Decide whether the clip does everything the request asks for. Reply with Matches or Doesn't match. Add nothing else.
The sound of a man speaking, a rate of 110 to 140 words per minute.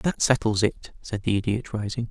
Doesn't match